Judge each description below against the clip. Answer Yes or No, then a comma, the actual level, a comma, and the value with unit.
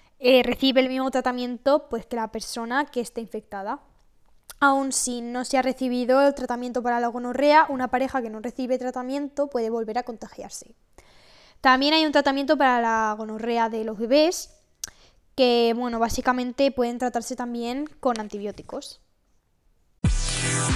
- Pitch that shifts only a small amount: Yes, narrow, 2.3 semitones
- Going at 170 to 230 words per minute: No, average, 145 wpm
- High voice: Yes, very high, 250 Hz